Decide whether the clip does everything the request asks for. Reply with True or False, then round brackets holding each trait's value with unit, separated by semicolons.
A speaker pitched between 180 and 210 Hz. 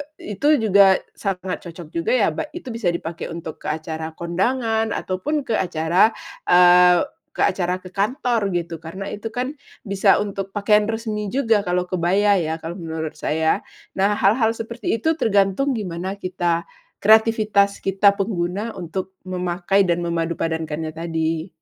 True (190 Hz)